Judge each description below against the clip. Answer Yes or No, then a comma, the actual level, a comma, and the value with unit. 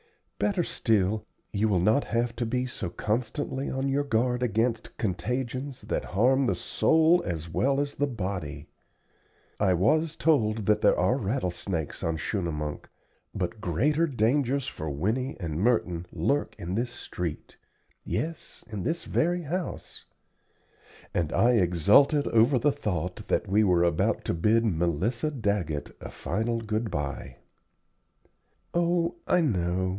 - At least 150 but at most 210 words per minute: No, average, 140 wpm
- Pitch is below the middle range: Yes, low, 110 Hz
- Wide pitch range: Yes, wide, 7.1 semitones